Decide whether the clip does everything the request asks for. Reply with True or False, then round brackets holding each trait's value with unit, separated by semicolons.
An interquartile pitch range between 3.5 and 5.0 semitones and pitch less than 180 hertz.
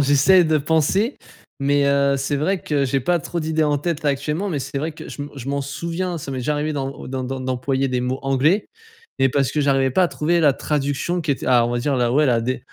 False (2.7 semitones; 140 Hz)